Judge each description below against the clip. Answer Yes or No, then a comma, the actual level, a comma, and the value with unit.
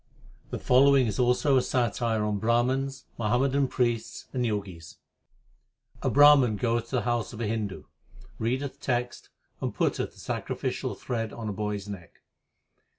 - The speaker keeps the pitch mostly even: No, average, 3.2 semitones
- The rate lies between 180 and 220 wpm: No, average, 150 wpm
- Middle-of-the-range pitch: No, low, 120 Hz